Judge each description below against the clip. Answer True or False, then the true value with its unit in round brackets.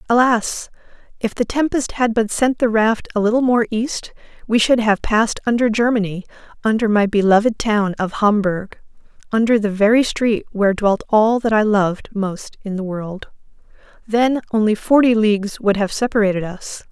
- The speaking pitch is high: True (215 Hz)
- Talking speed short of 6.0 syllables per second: True (5.0 syllables/s)